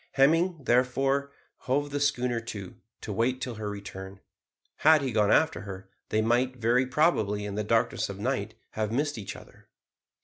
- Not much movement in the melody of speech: No, average, 4.6 semitones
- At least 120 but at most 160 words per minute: No, average, 170 wpm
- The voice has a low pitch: Yes, low, 120 Hz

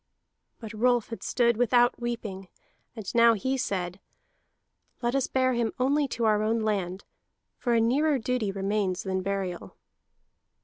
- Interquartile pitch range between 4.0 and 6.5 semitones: No, average, 3.6 semitones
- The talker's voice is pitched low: No, high, 230 Hz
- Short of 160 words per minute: Yes, average, 145 wpm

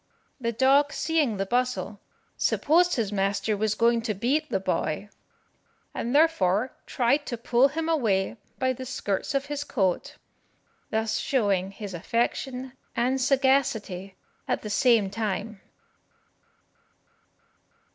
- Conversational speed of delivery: No, slow, 125 wpm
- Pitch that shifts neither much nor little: Yes, average, 4.9 semitones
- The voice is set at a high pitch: Yes, high, 235 Hz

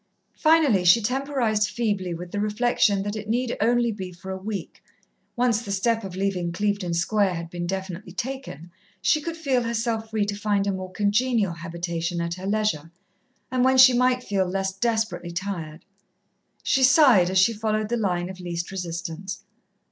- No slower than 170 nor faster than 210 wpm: Yes, average, 175 wpm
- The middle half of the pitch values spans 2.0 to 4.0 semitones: No, average, 4.5 semitones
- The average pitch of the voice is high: Yes, high, 205 Hz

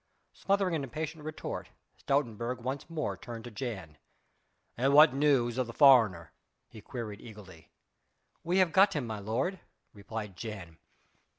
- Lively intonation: Yes, wide, 5.7 semitones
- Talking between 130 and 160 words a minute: Yes, average, 140 wpm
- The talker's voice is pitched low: Yes, low, 120 Hz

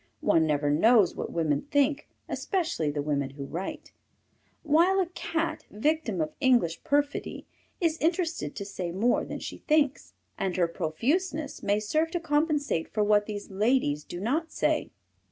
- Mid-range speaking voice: No, high, 230 Hz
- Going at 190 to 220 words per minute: No, average, 155 wpm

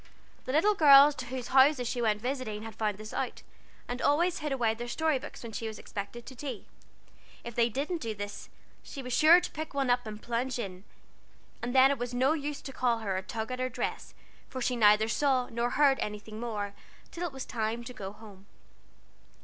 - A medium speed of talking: No, fast, 215 wpm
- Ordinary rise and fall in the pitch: Yes, average, 3.8 semitones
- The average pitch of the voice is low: No, high, 245 Hz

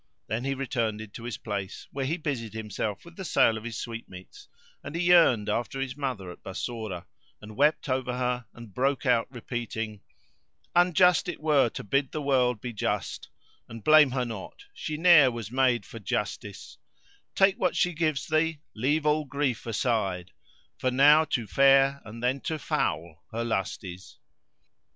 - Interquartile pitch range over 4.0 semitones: Yes, average, 4.8 semitones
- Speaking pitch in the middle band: No, low, 125 Hz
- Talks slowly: No, average, 180 wpm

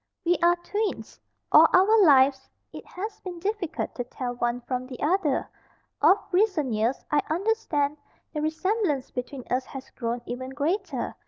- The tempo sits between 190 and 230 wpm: No, average, 155 wpm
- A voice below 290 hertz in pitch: No, very high, 300 Hz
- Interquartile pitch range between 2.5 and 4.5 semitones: No, wide, 6.4 semitones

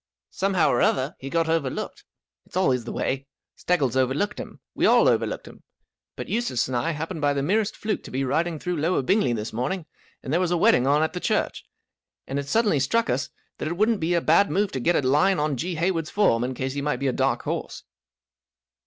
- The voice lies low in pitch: No, medium, 155 Hz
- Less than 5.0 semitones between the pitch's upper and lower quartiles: No, wide, 5.4 semitones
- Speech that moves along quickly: Yes, fast, 230 wpm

